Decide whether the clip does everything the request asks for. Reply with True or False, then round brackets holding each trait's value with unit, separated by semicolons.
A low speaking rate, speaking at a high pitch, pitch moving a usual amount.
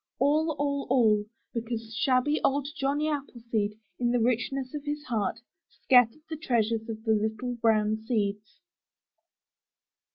True (130 wpm; 240 Hz; 4.1 semitones)